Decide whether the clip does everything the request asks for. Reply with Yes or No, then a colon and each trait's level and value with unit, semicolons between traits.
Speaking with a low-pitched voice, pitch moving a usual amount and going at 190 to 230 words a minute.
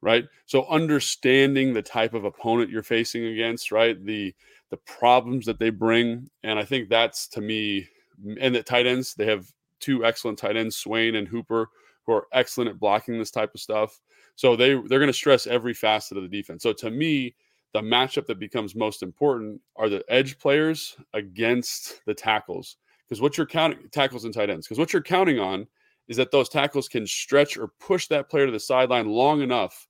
Yes: low, 120 Hz; average, 3.7 semitones; average, 200 wpm